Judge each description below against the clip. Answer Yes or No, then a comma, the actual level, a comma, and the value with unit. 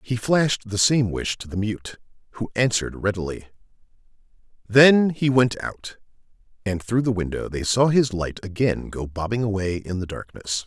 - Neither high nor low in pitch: No, low, 110 Hz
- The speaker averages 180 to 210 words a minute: No, average, 170 wpm